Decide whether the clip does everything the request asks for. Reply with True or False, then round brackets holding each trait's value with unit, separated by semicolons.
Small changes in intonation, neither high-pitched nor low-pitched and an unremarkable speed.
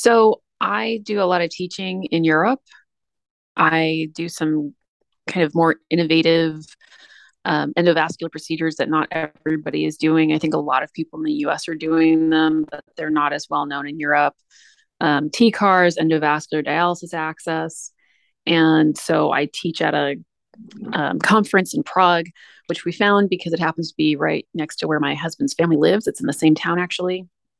True (2.3 semitones; 160 Hz; 175 wpm)